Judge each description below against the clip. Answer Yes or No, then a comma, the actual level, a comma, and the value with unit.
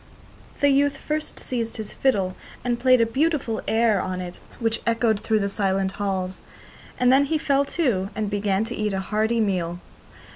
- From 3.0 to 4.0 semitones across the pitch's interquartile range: No, average, 4.6 semitones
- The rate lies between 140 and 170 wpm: No, average, 180 wpm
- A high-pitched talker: Yes, high, 220 Hz